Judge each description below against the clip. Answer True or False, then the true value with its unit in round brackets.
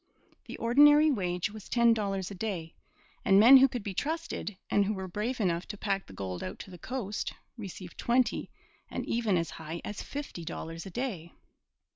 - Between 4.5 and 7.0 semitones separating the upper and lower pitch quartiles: True (5.1 semitones)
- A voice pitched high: True (205 Hz)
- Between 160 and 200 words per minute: True (190 wpm)